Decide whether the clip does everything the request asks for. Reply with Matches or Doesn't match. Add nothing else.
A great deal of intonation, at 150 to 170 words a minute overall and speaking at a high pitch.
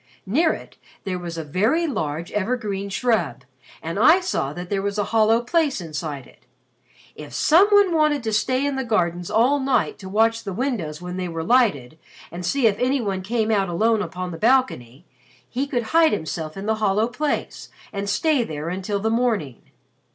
Doesn't match